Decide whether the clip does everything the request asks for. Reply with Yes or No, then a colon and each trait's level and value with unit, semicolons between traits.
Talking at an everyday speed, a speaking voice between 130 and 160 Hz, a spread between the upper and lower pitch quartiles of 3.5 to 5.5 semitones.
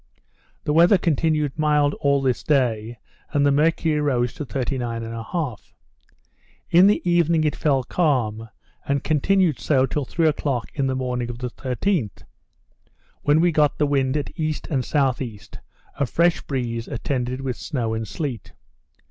Yes: average, 155 wpm; medium, 140 Hz; average, 3.8 semitones